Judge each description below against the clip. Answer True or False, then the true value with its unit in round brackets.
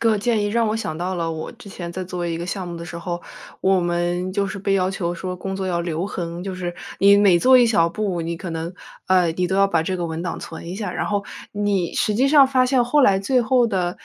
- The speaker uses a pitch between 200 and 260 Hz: False (185 Hz)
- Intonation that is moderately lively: True (3.0 semitones)